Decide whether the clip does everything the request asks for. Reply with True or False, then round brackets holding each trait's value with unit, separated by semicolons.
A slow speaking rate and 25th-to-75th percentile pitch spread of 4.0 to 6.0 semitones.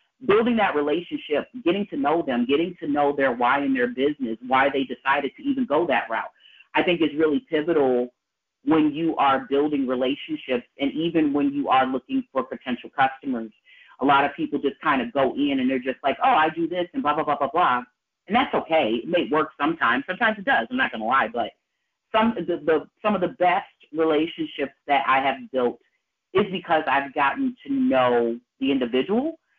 False (205 wpm; 4.8 semitones)